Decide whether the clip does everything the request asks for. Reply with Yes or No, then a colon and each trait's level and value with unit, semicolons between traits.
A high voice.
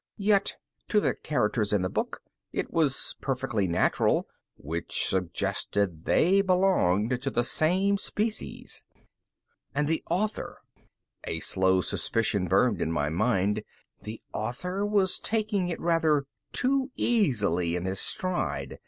No: low, 125 Hz